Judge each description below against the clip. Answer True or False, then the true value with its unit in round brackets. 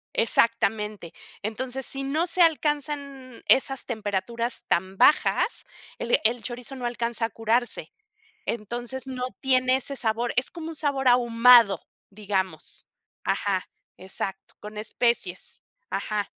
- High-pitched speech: True (240 Hz)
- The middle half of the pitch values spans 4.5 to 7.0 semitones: False (3.7 semitones)